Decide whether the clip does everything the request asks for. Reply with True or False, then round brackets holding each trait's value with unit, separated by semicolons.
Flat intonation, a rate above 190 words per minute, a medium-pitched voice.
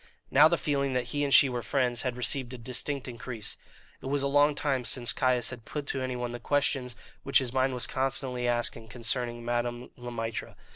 False (2.2 semitones; 205 wpm; 125 Hz)